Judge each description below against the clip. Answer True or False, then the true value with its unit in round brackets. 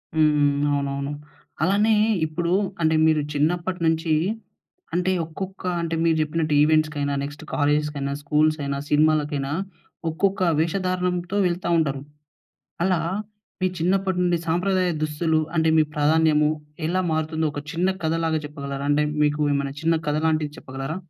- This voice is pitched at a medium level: True (155 Hz)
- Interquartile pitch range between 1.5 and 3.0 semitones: True (2.7 semitones)